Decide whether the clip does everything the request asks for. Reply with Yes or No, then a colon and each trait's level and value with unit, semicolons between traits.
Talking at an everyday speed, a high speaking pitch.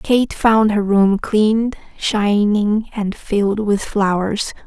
No: slow, 130 wpm; high, 210 Hz